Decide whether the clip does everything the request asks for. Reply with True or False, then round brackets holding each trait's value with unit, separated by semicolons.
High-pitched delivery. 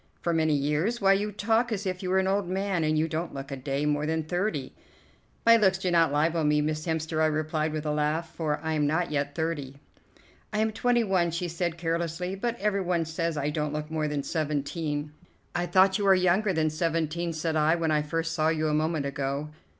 False (160 Hz)